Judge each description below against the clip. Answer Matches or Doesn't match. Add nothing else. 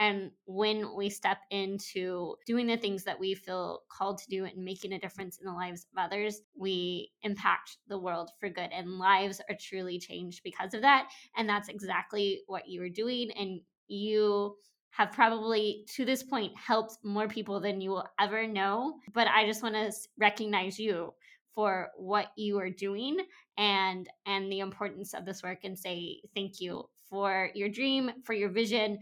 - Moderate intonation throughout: Doesn't match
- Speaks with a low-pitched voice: Doesn't match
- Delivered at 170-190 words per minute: Matches